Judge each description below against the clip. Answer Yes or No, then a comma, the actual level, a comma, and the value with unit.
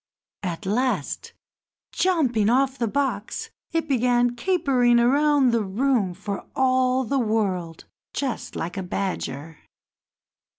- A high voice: Yes, high, 245 Hz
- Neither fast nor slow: No, slow, 115 wpm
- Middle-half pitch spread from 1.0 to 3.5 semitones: No, average, 5.0 semitones